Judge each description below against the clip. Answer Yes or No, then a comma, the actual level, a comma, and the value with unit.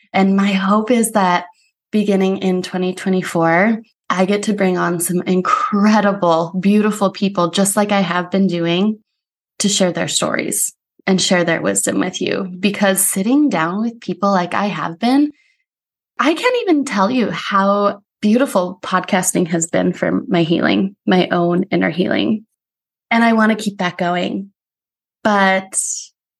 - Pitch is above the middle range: Yes, high, 195 Hz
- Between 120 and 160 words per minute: Yes, average, 150 wpm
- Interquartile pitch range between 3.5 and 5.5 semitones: No, average, 2.8 semitones